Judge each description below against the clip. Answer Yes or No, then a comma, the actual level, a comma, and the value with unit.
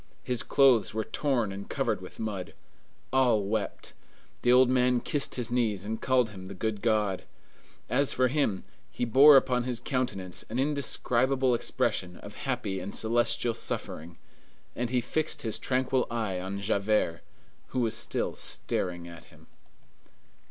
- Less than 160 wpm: Yes, average, 150 wpm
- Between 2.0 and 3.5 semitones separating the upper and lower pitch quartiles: No, average, 4.2 semitones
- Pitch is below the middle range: Yes, low, 115 Hz